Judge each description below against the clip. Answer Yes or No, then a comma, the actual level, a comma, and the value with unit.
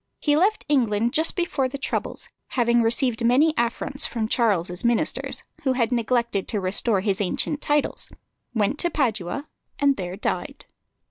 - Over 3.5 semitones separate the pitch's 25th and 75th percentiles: Yes, average, 4.5 semitones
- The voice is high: Yes, high, 235 Hz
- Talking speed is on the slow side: No, average, 150 wpm